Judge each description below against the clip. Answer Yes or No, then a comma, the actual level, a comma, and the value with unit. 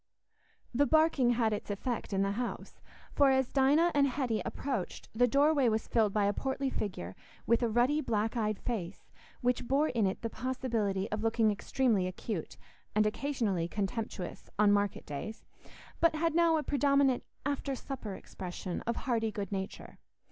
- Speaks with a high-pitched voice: Yes, high, 235 Hz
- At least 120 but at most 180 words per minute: Yes, average, 165 wpm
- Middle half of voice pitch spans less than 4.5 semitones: No, average, 4.8 semitones